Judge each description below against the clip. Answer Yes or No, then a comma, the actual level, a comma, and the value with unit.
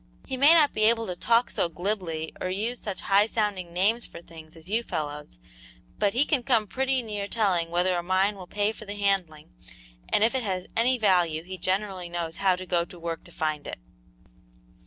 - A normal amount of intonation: Yes, average, 4.2 semitones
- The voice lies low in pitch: No, high, 195 Hz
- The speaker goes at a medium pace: No, fast, 210 wpm